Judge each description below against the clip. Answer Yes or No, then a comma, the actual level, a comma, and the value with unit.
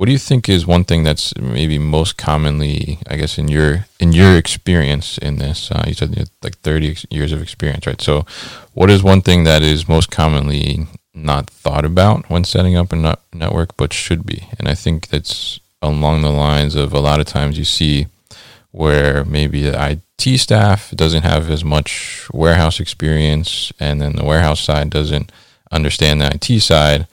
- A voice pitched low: Yes, very low, 80 Hz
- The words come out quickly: No, average, 190 wpm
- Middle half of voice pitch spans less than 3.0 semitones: No, average, 3.3 semitones